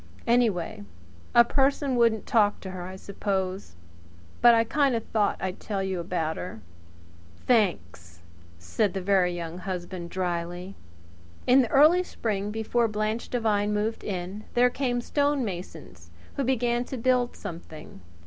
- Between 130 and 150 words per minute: Yes, average, 140 wpm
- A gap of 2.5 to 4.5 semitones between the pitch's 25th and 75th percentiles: No, average, 4.9 semitones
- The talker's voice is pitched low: No, high, 205 Hz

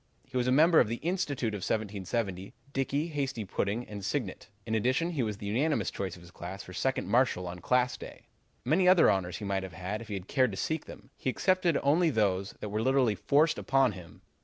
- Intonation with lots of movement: Yes, wide, 6.1 semitones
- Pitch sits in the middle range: No, low, 115 Hz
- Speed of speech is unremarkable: No, fast, 225 wpm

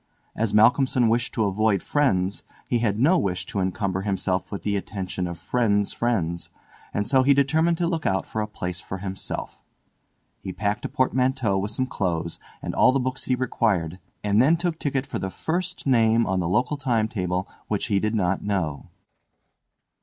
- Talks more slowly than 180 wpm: No, average, 185 wpm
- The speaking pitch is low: Yes, low, 105 Hz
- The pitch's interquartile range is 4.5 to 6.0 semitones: Yes, wide, 5.4 semitones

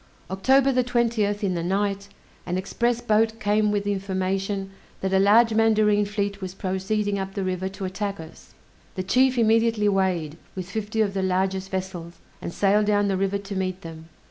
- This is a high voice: Yes, high, 200 Hz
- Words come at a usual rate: Yes, average, 185 wpm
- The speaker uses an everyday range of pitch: No, narrow, 2.0 semitones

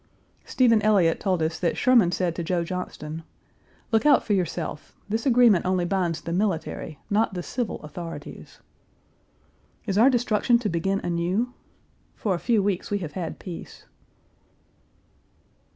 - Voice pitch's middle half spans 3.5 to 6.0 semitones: Yes, average, 4.4 semitones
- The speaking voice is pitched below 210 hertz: Yes, high, 190 Hz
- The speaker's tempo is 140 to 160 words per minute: Yes, average, 145 wpm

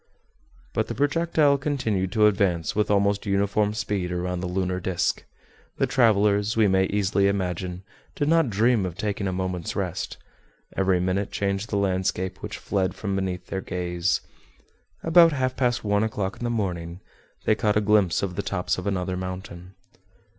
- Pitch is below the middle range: Yes, low, 100 Hz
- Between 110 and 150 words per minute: No, average, 170 wpm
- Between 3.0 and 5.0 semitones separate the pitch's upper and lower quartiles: No, narrow, 2.6 semitones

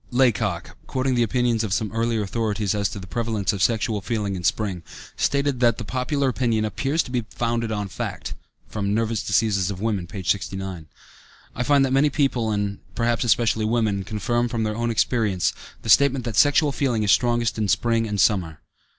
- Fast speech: No, average, 185 wpm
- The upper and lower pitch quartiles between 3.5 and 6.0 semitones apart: No, average, 3.0 semitones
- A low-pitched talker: Yes, low, 110 Hz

